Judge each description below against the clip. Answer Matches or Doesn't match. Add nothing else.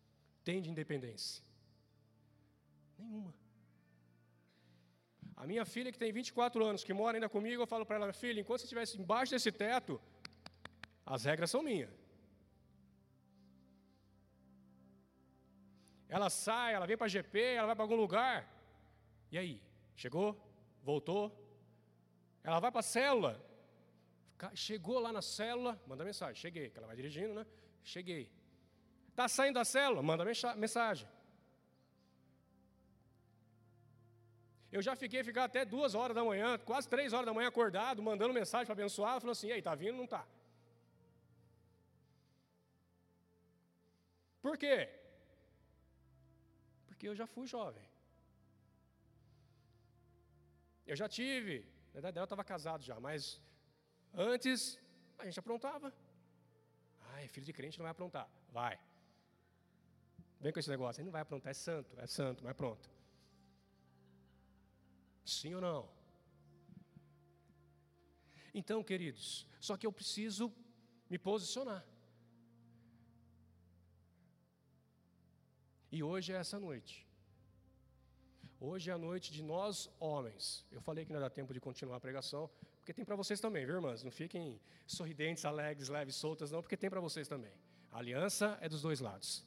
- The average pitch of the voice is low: Doesn't match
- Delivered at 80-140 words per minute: Matches